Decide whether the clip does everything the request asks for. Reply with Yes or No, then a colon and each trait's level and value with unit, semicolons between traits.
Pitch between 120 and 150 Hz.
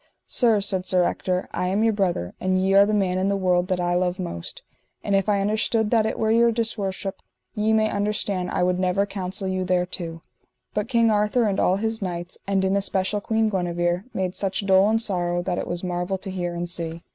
No: high, 190 Hz